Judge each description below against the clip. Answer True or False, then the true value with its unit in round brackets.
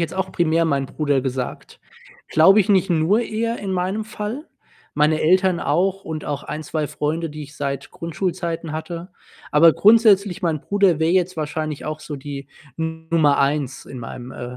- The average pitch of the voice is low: False (160 Hz)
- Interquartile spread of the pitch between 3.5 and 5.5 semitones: True (4.0 semitones)